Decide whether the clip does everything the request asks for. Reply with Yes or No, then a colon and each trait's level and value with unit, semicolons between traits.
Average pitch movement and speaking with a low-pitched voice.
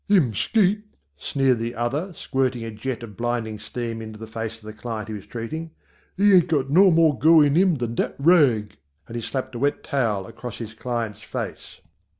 Yes: average, 5.0 semitones; low, 120 Hz